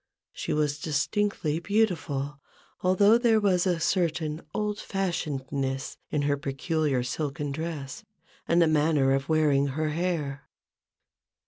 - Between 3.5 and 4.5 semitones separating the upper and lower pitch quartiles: Yes, average, 4.2 semitones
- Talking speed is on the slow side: Yes, slow, 120 wpm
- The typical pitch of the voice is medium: Yes, medium, 155 Hz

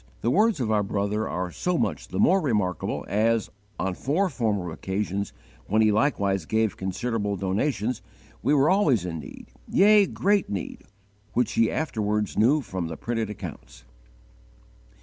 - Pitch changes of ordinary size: No, wide, 5.8 semitones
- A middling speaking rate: Yes, average, 150 wpm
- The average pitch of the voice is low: Yes, low, 110 Hz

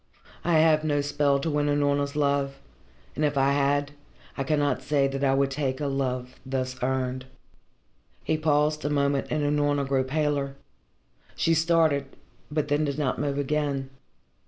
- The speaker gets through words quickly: No, average, 160 wpm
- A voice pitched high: No, medium, 145 Hz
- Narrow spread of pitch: Yes, narrow, 1.4 semitones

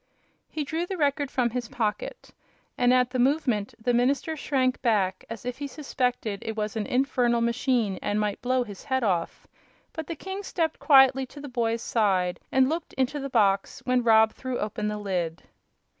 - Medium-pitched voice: No, high, 245 Hz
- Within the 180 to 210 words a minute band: Yes, average, 190 wpm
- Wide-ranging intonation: No, average, 4.0 semitones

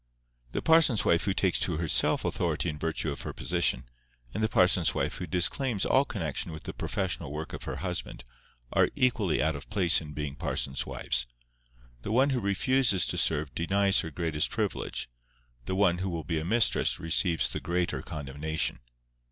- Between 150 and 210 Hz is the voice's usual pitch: No, very low, 85 Hz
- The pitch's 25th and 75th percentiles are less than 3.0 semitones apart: No, average, 4.3 semitones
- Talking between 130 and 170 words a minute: No, average, 180 wpm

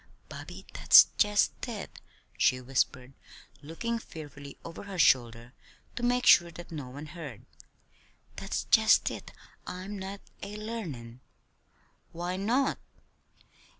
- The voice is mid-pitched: Yes, medium, 170 Hz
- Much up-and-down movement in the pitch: Yes, wide, 7.3 semitones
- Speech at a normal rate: No, slow, 115 wpm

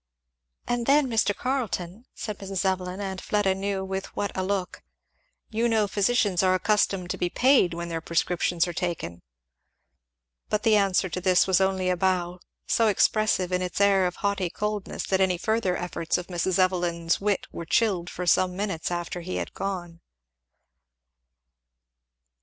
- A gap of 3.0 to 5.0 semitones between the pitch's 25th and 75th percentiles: No, narrow, 2.4 semitones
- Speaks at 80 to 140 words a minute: No, average, 165 wpm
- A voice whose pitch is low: No, high, 190 Hz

